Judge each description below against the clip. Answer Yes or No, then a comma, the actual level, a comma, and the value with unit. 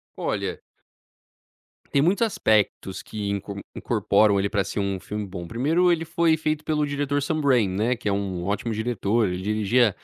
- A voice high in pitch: No, low, 110 Hz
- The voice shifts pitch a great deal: Yes, wide, 6.3 semitones